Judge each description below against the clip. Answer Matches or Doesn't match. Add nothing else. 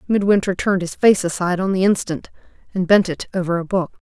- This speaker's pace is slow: Doesn't match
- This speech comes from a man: Doesn't match